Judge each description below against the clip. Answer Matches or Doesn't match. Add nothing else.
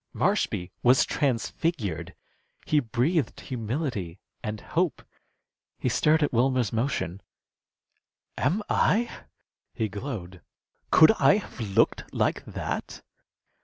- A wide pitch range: Matches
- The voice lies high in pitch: Doesn't match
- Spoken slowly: Matches